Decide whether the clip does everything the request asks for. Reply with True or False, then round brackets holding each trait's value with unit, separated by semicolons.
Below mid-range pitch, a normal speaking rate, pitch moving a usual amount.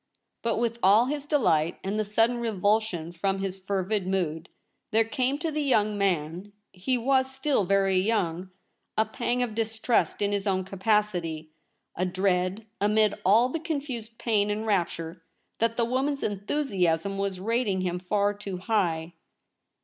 False (205 Hz; 160 wpm; 3.7 semitones)